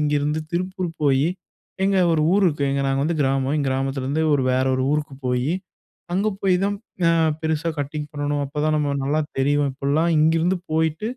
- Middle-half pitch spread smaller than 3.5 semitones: Yes, average, 2.7 semitones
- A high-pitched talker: No, medium, 150 Hz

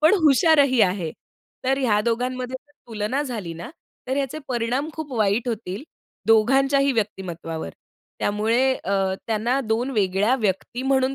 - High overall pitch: Yes, high, 235 Hz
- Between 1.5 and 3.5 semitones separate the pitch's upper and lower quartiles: No, average, 4.5 semitones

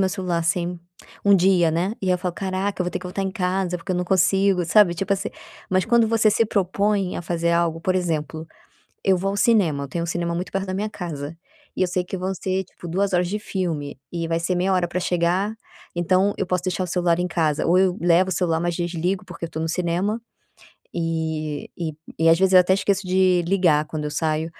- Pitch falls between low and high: Yes, medium, 180 Hz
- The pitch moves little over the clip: Yes, narrow, 2.1 semitones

